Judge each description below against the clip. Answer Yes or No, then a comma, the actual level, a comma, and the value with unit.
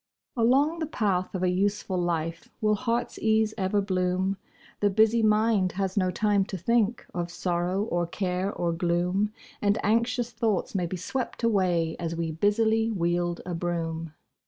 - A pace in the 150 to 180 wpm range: Yes, average, 160 wpm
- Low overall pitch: No, high, 190 Hz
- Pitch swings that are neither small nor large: Yes, average, 3.8 semitones